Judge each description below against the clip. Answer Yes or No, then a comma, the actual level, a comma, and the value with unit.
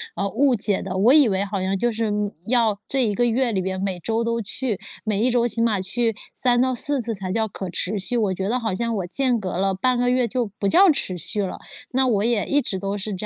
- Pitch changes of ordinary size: Yes, average, 3.8 semitones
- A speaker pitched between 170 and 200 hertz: No, high, 220 Hz